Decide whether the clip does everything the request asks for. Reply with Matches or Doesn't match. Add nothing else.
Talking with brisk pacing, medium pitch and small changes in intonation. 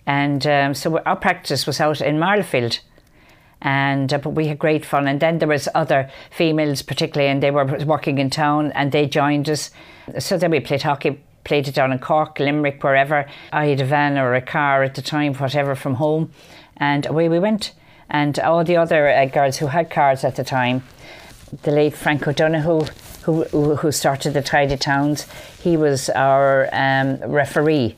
Doesn't match